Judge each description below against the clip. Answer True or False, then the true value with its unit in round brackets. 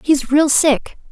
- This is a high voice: True (285 Hz)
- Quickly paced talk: False (160 wpm)